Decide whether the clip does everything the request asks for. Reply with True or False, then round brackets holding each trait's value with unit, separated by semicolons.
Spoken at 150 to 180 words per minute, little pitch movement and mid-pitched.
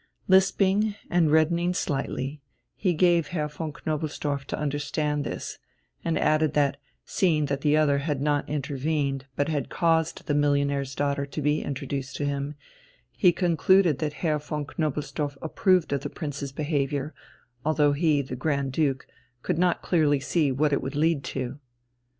True (155 wpm; 2.2 semitones; 150 Hz)